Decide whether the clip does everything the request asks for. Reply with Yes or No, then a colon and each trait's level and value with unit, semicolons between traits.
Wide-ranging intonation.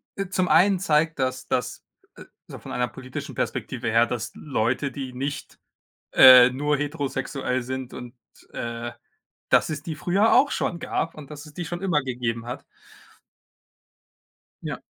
No: average, 4.3 semitones